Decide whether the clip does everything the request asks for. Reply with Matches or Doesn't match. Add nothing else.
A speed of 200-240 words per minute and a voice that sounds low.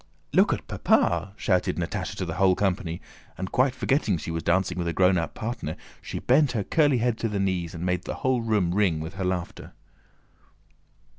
Matches